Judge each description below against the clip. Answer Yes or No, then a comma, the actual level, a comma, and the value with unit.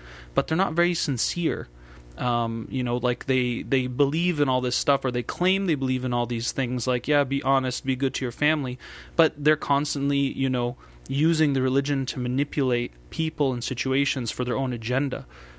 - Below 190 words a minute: No, average, 195 wpm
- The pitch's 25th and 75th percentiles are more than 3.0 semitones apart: No, narrow, 2.5 semitones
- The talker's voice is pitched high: No, low, 135 Hz